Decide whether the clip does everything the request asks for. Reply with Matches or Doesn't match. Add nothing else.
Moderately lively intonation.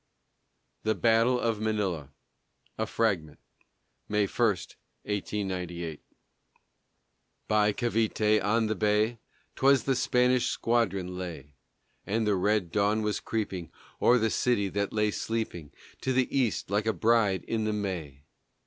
Matches